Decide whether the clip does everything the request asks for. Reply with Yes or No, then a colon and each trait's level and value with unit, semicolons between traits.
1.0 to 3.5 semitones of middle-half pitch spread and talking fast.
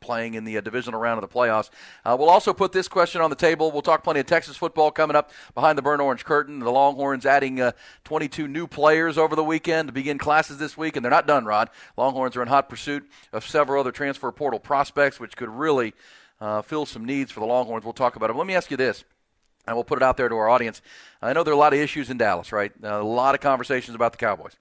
No: average, 4.2 semitones; fast, 265 wpm